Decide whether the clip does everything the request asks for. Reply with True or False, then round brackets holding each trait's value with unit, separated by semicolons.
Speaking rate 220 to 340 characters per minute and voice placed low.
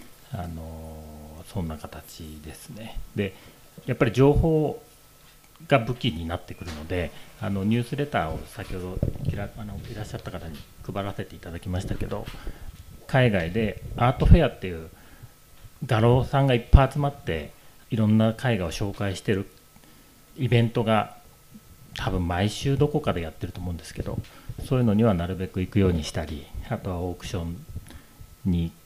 True (335 characters per minute; 100 Hz)